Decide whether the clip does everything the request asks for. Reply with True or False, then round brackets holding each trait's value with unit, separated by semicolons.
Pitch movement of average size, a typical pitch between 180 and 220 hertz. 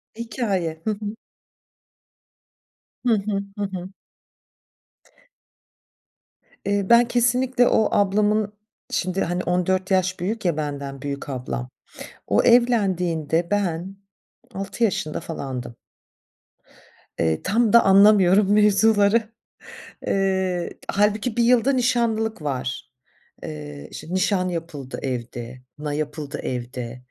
False (6.1 semitones; 190 Hz)